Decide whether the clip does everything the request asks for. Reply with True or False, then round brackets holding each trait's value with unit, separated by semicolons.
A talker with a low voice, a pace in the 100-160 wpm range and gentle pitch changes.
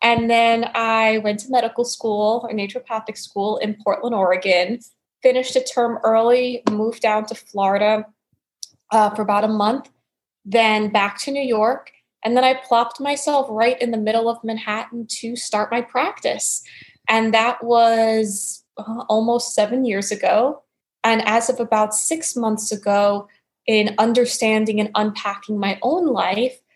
False (225 Hz; 155 wpm; 2.1 semitones)